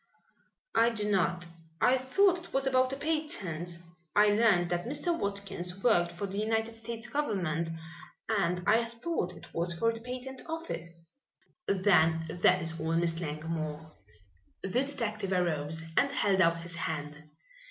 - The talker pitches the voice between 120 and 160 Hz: No, high, 195 Hz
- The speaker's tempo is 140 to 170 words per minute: Yes, average, 150 wpm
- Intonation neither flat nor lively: No, wide, 5.8 semitones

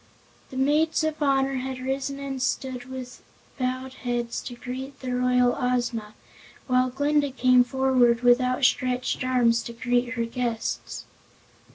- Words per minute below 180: Yes, average, 140 wpm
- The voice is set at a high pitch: Yes, very high, 255 Hz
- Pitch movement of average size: No, narrow, 1.4 semitones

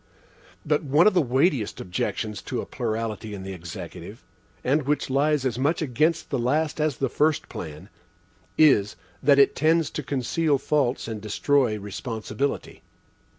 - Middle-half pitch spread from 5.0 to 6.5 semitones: Yes, average, 5.3 semitones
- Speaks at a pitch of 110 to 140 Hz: Yes, low, 135 Hz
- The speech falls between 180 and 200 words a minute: No, average, 150 wpm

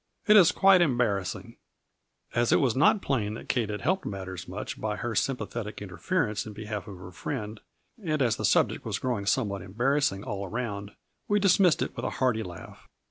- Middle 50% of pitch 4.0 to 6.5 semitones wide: Yes, average, 5.2 semitones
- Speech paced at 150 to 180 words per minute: No, average, 190 wpm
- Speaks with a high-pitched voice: No, low, 110 Hz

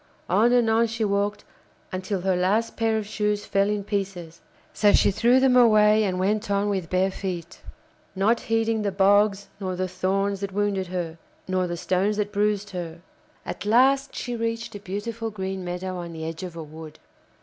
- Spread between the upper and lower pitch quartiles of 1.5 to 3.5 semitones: Yes, narrow, 2.5 semitones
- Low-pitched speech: No, high, 200 Hz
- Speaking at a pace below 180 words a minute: No, average, 190 wpm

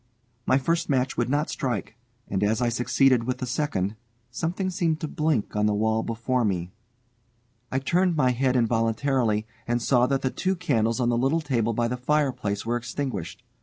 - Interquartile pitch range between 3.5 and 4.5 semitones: Yes, average, 3.8 semitones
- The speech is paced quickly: No, average, 185 wpm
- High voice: No, low, 125 Hz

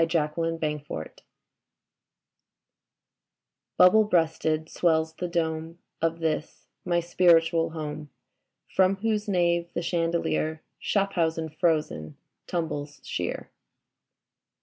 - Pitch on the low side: No, medium, 165 Hz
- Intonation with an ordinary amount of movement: No, narrow, 1.5 semitones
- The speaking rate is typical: No, slow, 95 wpm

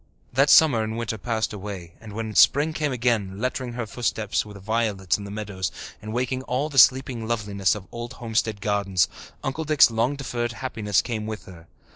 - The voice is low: Yes, low, 110 Hz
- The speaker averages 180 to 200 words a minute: Yes, average, 185 wpm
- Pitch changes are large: No, average, 3.3 semitones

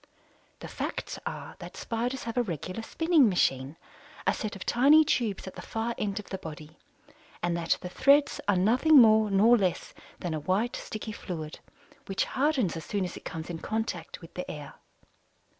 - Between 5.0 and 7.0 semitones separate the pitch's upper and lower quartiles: Yes, wide, 5.4 semitones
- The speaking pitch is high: Yes, high, 205 Hz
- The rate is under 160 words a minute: No, average, 185 wpm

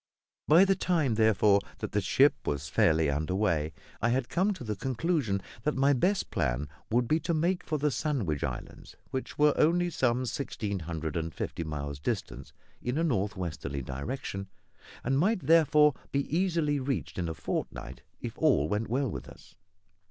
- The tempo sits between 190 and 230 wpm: No, average, 175 wpm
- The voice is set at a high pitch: No, low, 120 Hz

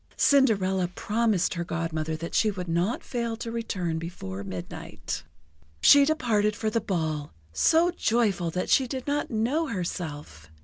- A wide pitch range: Yes, wide, 5.9 semitones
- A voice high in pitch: Yes, high, 195 Hz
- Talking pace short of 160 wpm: Yes, average, 145 wpm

